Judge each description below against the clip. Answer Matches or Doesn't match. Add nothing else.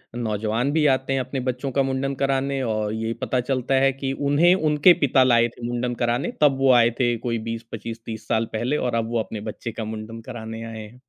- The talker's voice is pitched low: Matches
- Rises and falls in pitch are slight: Doesn't match